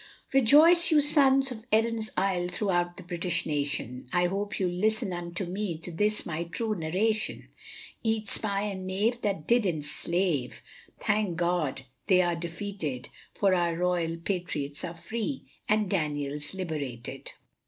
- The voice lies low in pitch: No, medium, 180 Hz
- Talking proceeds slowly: No, average, 145 wpm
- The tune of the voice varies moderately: Yes, average, 4.2 semitones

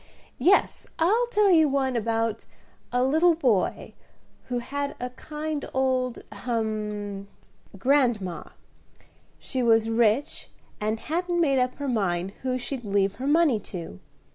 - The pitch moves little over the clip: No, average, 5.0 semitones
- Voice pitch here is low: No, very high, 250 Hz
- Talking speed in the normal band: No, slow, 130 wpm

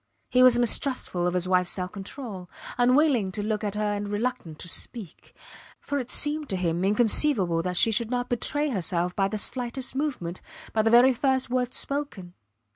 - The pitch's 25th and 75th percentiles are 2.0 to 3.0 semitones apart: No, wide, 5.6 semitones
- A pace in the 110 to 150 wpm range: No, average, 185 wpm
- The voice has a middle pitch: No, high, 220 Hz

